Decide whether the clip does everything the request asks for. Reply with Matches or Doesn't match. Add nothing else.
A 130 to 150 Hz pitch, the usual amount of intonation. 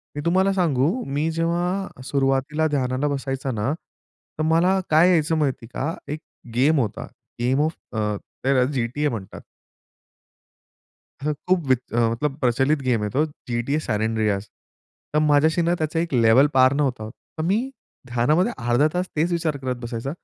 Matches